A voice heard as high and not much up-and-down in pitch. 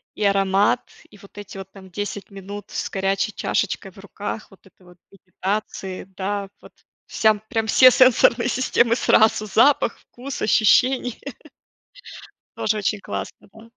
Yes: high, 205 Hz; narrow, 2.3 semitones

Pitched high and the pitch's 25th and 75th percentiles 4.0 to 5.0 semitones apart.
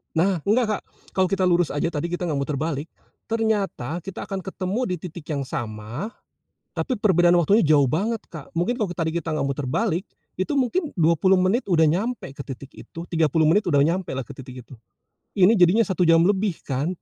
No: medium, 175 Hz; average, 4.6 semitones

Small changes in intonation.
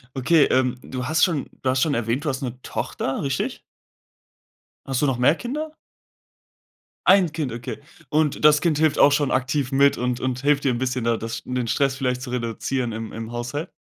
No: average, 3.0 semitones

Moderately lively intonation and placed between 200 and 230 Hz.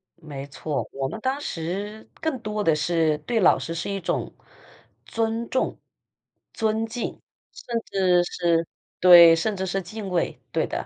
No: average, 5.0 semitones; high, 190 Hz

